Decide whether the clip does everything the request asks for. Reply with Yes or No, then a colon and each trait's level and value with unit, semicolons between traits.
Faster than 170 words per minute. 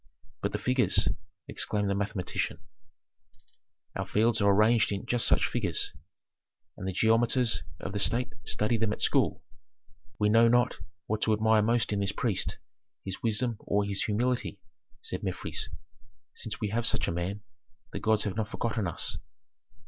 No: average, 160 wpm